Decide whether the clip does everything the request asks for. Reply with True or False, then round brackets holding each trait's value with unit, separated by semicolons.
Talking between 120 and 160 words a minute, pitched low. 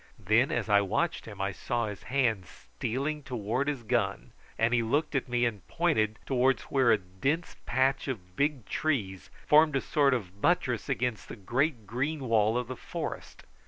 False (180 wpm; 120 Hz)